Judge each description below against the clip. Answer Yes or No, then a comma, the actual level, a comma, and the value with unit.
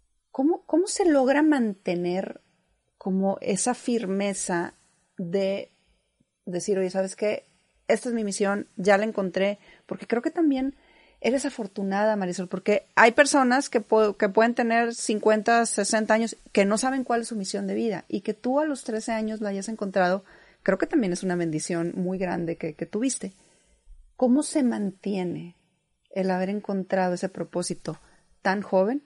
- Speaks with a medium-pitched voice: No, high, 205 Hz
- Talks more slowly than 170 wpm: Yes, average, 160 wpm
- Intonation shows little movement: No, average, 3.8 semitones